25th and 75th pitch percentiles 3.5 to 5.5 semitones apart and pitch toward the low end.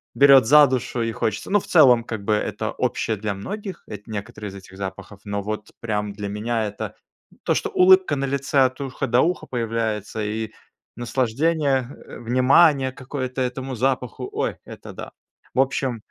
Yes: average, 4.1 semitones; low, 120 Hz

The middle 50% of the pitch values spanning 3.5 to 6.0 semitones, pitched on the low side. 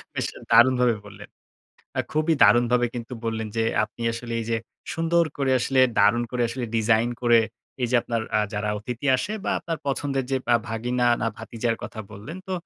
No: narrow, 2.5 semitones; low, 120 Hz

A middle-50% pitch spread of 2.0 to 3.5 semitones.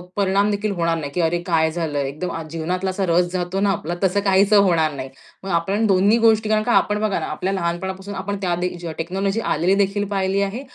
Yes: average, 2.8 semitones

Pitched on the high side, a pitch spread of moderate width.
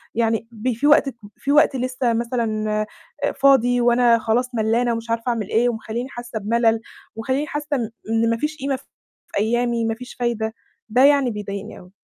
No: high, 235 Hz; narrow, 2.1 semitones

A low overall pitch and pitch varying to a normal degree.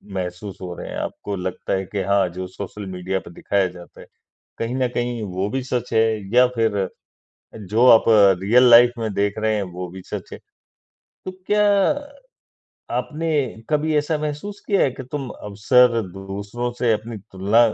Yes: low, 110 Hz; average, 4.6 semitones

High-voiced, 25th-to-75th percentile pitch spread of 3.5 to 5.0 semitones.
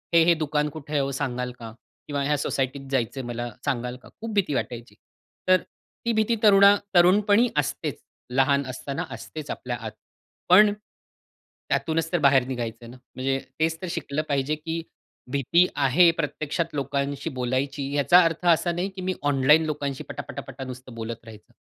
No: medium, 145 Hz; average, 4.1 semitones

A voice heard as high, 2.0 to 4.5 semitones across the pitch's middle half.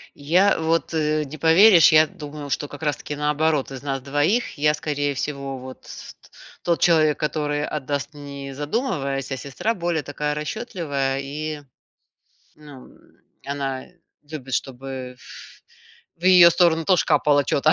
No: medium, 150 Hz; narrow, 2.5 semitones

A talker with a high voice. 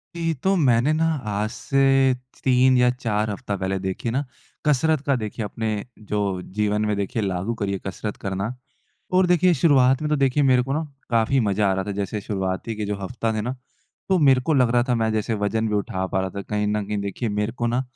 No: low, 110 Hz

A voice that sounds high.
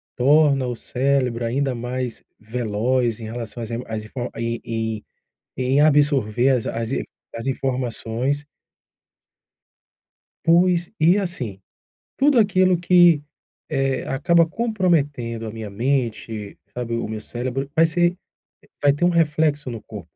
No: low, 130 Hz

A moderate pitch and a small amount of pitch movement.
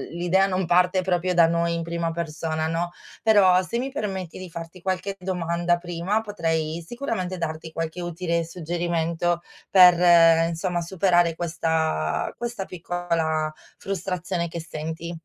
Yes: medium, 170 Hz; narrow, 1.9 semitones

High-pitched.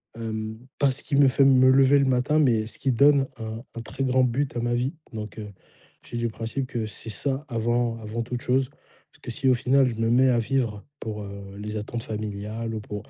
No: low, 120 Hz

